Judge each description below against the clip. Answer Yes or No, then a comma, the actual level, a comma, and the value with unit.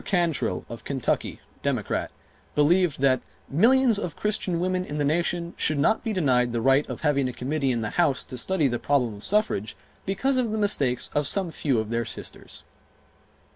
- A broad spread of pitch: Yes, wide, 6.5 semitones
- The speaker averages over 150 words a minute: Yes, average, 185 wpm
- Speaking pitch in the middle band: Yes, medium, 150 Hz